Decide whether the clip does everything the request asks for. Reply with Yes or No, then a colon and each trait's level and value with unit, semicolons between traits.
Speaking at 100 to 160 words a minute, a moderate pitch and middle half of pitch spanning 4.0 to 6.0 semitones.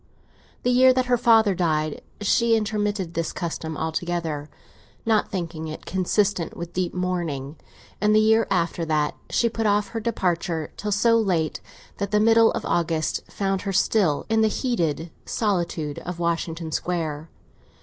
Yes: average, 155 wpm; medium, 180 Hz; average, 4.7 semitones